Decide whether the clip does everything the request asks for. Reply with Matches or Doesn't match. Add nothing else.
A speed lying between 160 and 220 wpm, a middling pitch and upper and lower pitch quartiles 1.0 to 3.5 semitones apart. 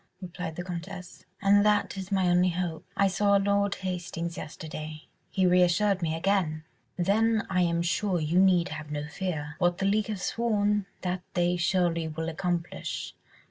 Matches